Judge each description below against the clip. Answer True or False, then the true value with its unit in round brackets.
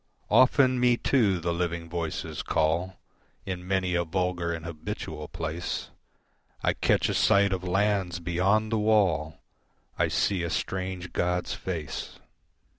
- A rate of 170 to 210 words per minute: False (135 wpm)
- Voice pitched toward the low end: True (90 Hz)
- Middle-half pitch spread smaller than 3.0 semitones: True (2.6 semitones)